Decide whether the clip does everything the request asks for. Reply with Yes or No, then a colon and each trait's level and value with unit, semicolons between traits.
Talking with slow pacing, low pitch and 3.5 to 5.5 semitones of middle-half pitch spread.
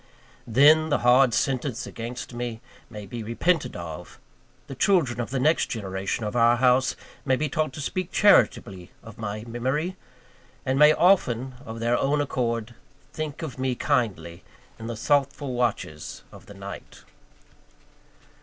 No: average, 150 wpm; low, 125 Hz; average, 3.9 semitones